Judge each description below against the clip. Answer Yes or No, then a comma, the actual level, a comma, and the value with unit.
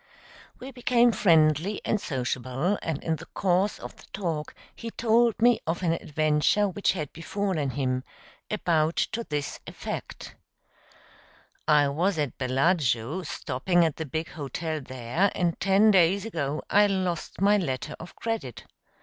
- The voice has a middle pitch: Yes, medium, 165 Hz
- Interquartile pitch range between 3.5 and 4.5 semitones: No, average, 5.3 semitones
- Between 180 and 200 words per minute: No, average, 145 wpm